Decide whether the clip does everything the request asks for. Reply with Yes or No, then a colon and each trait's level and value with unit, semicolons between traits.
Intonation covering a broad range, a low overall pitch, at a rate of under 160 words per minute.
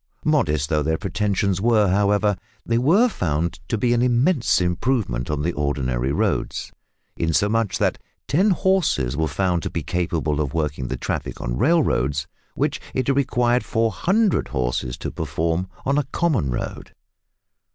Yes: wide, 8.8 semitones; very low, 95 Hz; average, 150 wpm